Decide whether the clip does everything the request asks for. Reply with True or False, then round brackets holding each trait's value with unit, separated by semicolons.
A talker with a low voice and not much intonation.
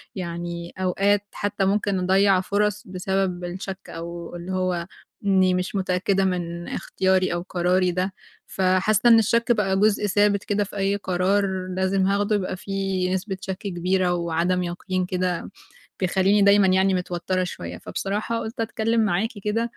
False (190 Hz; 1.8 semitones)